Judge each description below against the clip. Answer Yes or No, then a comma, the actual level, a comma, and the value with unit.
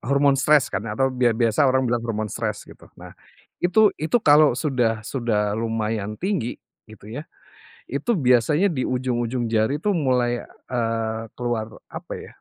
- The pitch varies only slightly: No, average, 3.7 semitones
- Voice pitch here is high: No, low, 120 Hz